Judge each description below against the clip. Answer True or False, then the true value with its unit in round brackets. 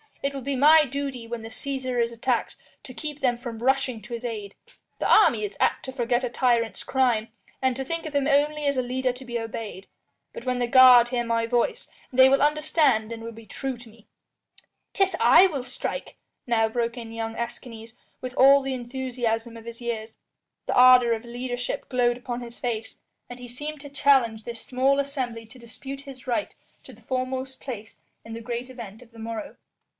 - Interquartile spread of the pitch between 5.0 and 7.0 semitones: False (2.6 semitones)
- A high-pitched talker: True (245 Hz)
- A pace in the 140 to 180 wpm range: False (205 wpm)